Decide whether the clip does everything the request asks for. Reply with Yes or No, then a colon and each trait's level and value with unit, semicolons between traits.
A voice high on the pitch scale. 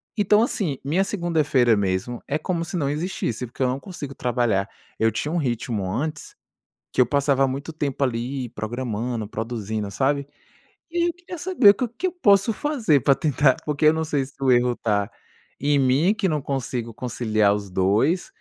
No: low, 135 Hz